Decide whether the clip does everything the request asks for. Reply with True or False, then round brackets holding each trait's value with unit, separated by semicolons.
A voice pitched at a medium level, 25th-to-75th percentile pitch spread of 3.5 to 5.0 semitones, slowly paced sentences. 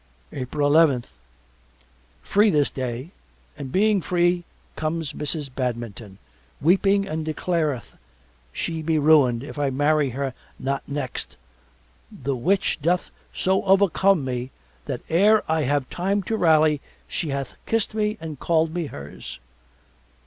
True (155 Hz; 4.6 semitones; 130 wpm)